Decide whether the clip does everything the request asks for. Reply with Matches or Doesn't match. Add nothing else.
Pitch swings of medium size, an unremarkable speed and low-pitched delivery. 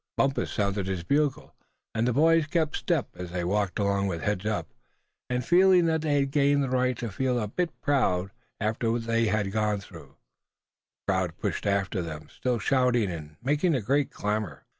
Doesn't match